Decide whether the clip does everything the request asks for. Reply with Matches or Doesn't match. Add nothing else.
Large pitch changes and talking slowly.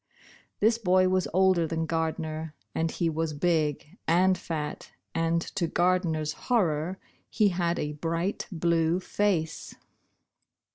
Doesn't match